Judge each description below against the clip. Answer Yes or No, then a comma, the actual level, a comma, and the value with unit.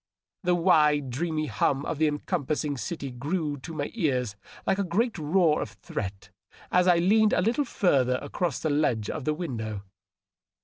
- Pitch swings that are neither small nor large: Yes, average, 5.0 semitones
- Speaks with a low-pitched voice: No, medium, 150 Hz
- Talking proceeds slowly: No, average, 170 wpm